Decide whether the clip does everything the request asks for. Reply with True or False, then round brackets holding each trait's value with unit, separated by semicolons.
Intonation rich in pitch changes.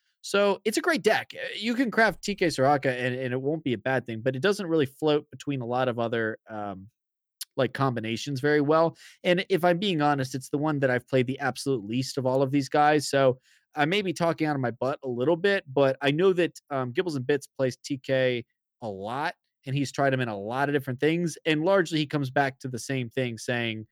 False (3.6 semitones)